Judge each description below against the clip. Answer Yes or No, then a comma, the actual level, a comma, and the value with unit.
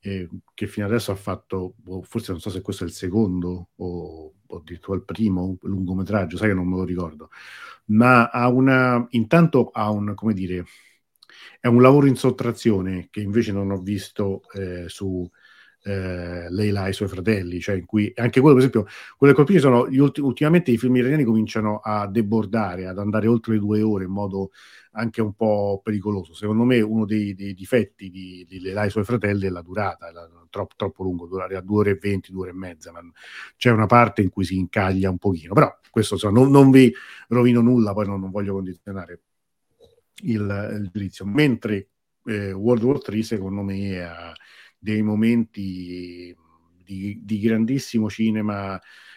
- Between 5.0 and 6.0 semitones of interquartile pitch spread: No, average, 3.4 semitones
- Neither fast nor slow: No, fast, 185 wpm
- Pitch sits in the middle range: No, low, 105 Hz